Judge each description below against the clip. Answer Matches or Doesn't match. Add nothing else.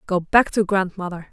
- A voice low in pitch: Doesn't match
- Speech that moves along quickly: Doesn't match